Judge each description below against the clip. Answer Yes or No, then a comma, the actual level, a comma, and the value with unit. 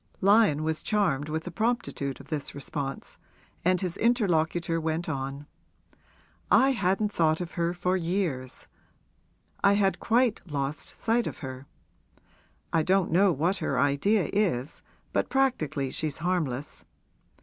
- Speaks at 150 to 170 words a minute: No, slow, 135 wpm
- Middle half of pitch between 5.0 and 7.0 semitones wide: Yes, wide, 5.5 semitones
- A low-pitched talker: No, medium, 170 Hz